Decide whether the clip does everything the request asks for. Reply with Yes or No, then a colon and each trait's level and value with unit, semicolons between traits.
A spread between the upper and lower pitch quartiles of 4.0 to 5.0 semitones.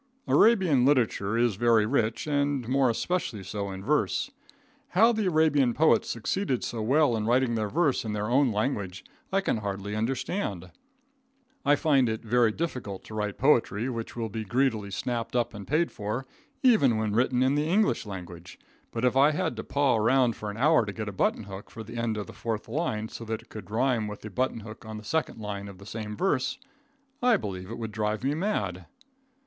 Yes: average, 4.7 semitones